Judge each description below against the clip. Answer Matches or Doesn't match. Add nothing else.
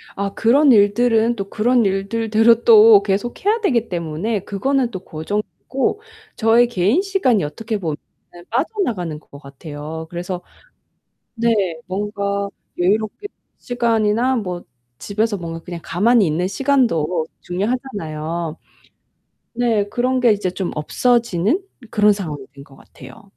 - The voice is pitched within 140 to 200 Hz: Doesn't match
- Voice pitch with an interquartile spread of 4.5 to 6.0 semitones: Matches